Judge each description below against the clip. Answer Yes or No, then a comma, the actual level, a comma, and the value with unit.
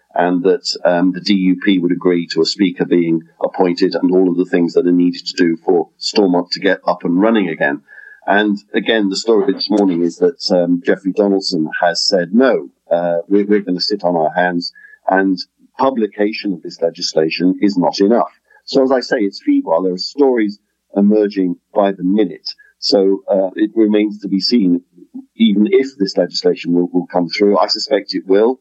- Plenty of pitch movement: No, average, 3.2 semitones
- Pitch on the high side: No, very low, 95 Hz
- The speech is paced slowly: No, average, 200 wpm